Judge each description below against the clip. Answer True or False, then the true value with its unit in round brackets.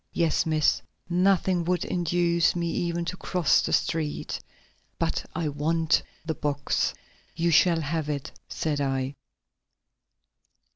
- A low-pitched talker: False (165 Hz)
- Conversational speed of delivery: False (125 wpm)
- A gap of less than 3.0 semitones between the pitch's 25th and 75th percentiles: True (2.5 semitones)